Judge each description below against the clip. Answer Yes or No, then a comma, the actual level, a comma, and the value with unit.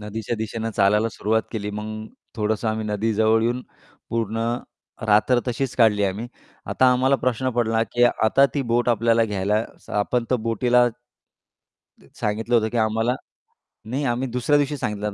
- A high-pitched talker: No, low, 115 Hz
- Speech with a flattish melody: Yes, narrow, 2.3 semitones